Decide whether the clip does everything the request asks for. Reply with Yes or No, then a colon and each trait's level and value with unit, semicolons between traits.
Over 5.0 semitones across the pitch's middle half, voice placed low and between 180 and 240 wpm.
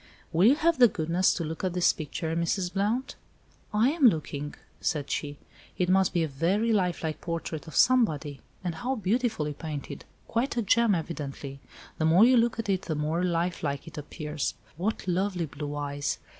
No: wide, 5.6 semitones; medium, 170 Hz; average, 185 wpm